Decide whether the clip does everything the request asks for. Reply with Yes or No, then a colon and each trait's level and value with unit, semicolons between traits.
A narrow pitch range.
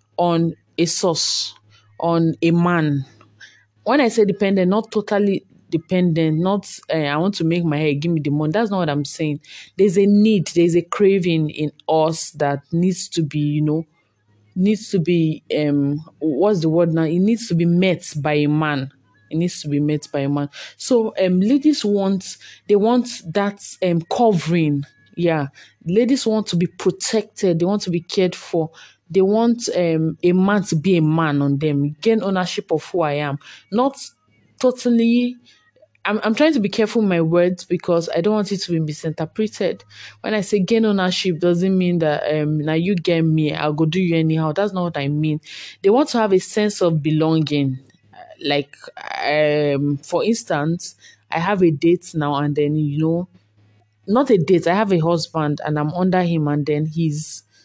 No: average, 4.6 semitones